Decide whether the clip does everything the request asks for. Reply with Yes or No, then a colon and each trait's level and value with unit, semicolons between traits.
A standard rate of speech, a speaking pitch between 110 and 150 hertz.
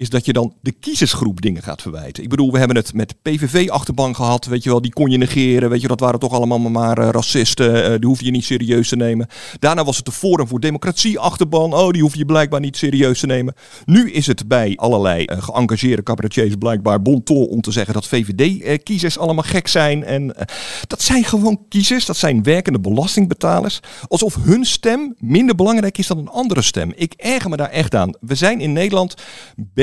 No: fast, 215 wpm; low, 135 Hz